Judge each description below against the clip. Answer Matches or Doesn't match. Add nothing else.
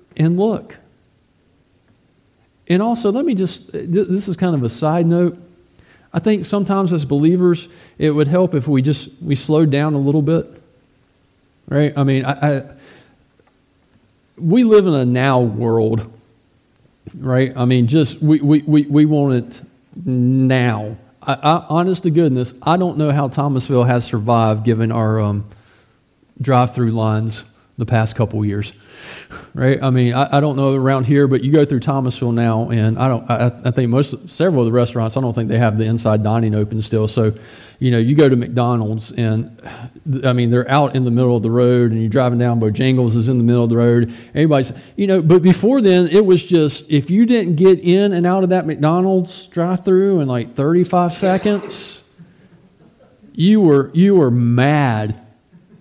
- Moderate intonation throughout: Doesn't match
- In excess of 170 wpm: Matches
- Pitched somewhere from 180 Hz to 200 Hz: Doesn't match